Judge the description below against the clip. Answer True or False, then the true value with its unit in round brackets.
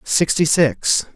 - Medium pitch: True (150 Hz)